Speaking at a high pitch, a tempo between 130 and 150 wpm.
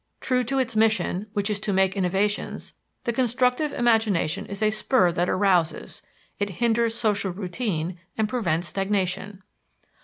Yes: high, 205 Hz; average, 145 wpm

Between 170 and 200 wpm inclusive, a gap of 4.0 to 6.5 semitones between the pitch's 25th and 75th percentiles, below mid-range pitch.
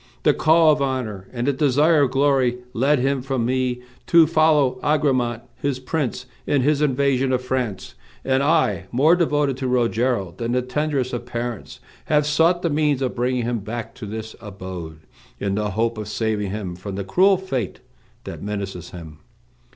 Yes: average, 175 wpm; average, 4.7 semitones; low, 125 Hz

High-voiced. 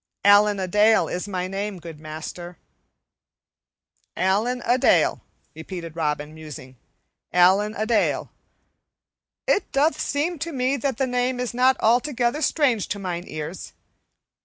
Yes: high, 210 Hz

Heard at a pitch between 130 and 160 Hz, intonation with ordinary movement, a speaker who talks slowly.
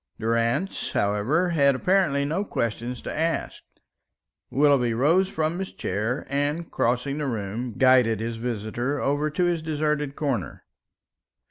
Yes: medium, 140 Hz; average, 4.8 semitones; slow, 130 wpm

